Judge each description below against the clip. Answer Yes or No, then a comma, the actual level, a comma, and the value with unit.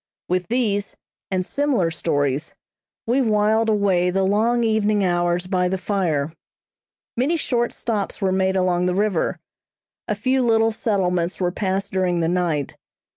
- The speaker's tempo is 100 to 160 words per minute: Yes, average, 145 wpm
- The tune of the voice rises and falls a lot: No, average, 3.5 semitones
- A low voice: No, high, 190 Hz